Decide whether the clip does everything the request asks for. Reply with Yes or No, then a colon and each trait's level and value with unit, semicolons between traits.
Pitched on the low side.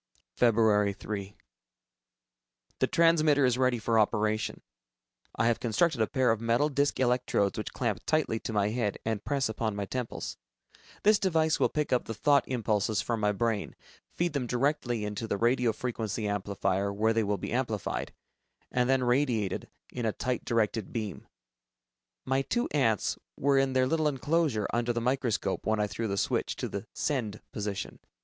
Yes: low, 115 Hz